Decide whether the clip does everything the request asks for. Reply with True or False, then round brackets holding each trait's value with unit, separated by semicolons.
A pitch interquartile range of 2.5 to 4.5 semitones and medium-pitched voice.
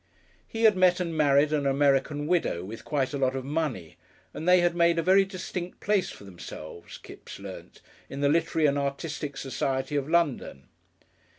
True (4.0 semitones; 150 Hz)